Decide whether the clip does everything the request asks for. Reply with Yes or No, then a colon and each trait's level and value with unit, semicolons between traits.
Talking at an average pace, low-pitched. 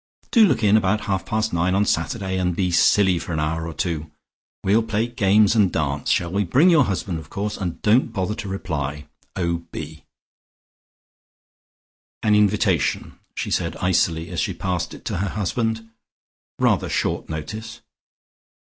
Yes: average, 160 wpm; very low, 95 Hz